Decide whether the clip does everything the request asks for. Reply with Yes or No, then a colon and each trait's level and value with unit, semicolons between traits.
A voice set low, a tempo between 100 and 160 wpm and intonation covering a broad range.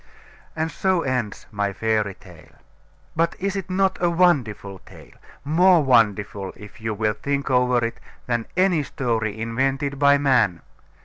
Yes: low, 125 Hz; average, 145 wpm; wide, 6.7 semitones